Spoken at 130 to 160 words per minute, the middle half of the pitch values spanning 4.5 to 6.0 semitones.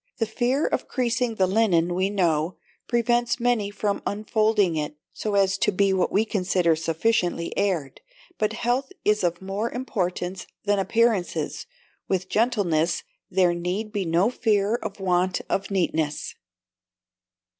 No: average, 140 wpm; average, 3.8 semitones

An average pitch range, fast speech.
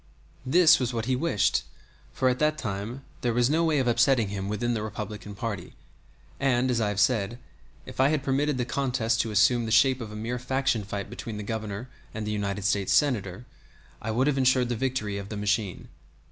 Yes: average, 3.9 semitones; fast, 210 wpm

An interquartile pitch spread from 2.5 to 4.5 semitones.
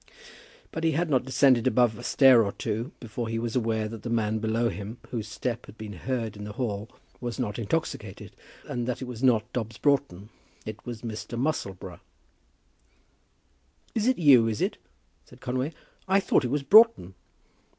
Yes: average, 3.2 semitones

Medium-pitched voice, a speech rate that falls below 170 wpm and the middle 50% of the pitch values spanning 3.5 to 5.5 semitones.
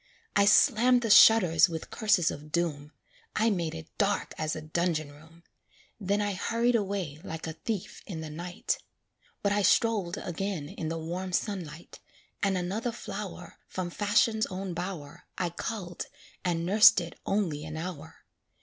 Yes: medium, 180 Hz; average, 160 wpm; average, 4.1 semitones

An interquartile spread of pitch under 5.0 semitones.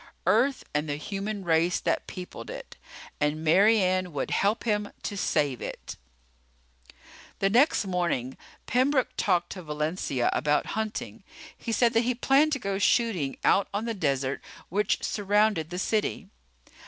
No: wide, 5.6 semitones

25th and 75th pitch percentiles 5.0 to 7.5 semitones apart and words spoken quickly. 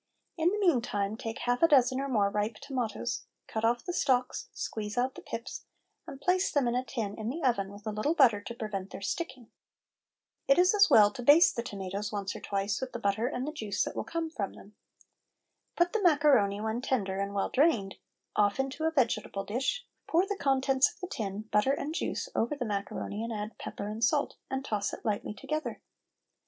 Yes: wide, 5.4 semitones; fast, 210 wpm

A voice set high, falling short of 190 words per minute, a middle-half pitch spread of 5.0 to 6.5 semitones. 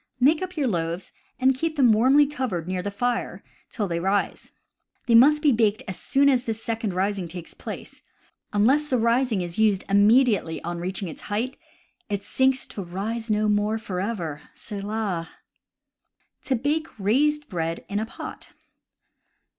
Yes: high, 215 Hz; average, 170 wpm; average, 5.3 semitones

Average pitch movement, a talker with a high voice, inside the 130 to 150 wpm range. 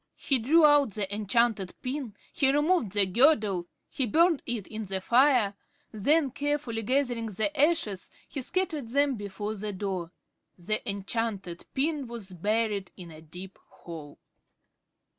No: wide, 6.2 semitones; high, 225 Hz; average, 140 wpm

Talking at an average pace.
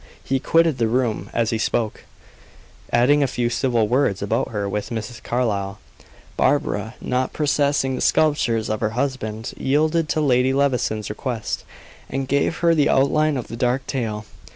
Yes: average, 160 wpm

